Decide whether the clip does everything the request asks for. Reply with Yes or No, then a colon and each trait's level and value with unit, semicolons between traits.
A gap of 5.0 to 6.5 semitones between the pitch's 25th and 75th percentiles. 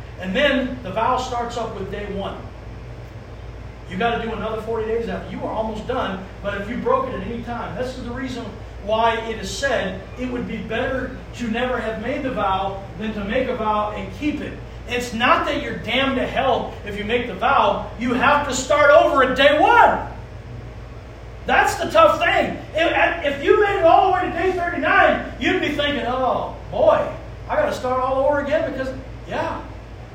Yes: wide, 5.4 semitones